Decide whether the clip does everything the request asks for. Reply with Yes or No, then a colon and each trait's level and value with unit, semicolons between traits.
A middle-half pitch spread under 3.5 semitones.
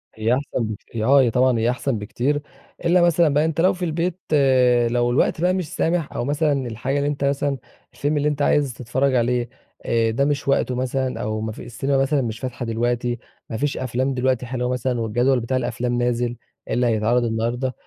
Yes: average, 2.9 semitones